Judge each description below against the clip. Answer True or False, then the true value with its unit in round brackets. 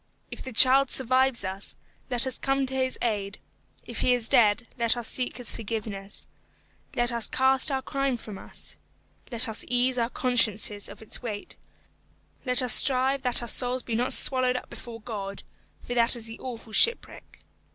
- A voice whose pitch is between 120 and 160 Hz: False (245 Hz)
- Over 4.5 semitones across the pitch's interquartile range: False (2.6 semitones)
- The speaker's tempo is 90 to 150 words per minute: False (180 wpm)